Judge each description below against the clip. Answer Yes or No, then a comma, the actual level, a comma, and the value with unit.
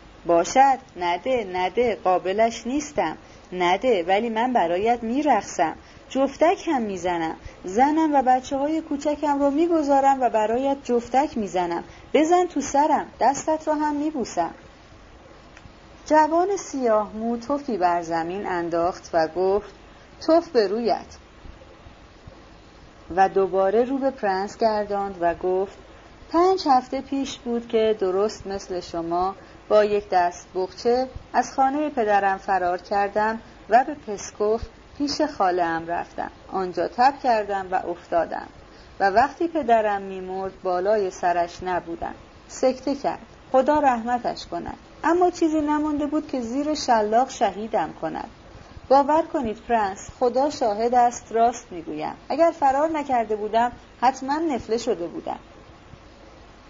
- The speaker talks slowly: No, average, 125 wpm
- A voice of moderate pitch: No, high, 235 Hz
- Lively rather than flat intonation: Yes, wide, 6.7 semitones